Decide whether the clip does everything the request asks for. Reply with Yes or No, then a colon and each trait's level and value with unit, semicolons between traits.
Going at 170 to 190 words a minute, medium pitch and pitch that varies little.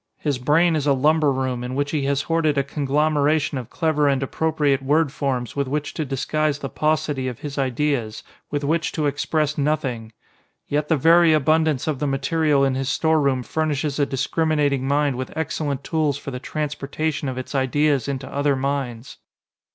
Yes: average, 180 wpm; medium, 145 Hz; narrow, 2.3 semitones